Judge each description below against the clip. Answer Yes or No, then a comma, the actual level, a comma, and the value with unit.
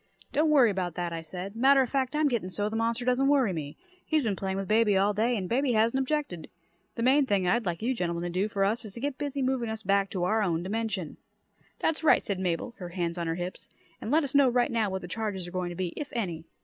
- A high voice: Yes, high, 215 Hz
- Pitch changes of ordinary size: No, wide, 5.7 semitones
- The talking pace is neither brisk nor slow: No, fast, 265 wpm